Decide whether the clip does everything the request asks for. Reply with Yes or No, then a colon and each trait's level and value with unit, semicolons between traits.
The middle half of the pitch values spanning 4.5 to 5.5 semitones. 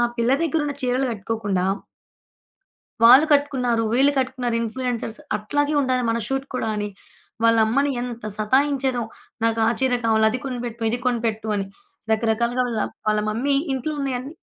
No: average, 2.8 semitones